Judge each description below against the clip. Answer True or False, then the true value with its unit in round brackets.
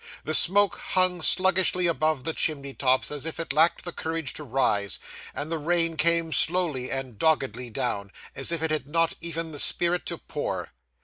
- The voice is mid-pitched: True (160 Hz)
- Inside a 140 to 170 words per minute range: False (185 wpm)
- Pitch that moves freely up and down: False (3.7 semitones)